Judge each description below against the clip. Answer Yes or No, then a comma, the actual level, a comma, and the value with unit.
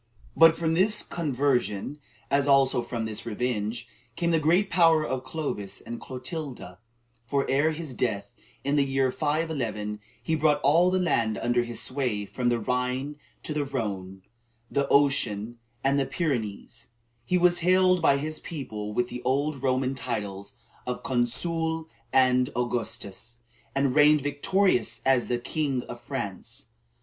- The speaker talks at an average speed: Yes, average, 150 wpm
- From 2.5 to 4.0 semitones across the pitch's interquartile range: No, average, 4.5 semitones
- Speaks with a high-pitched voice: No, low, 135 Hz